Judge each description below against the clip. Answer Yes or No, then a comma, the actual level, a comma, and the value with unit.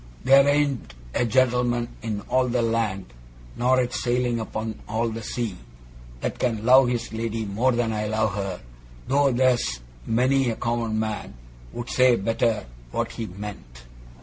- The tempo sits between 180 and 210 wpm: No, average, 155 wpm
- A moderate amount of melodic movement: No, narrow, 2.3 semitones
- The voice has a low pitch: Yes, low, 115 Hz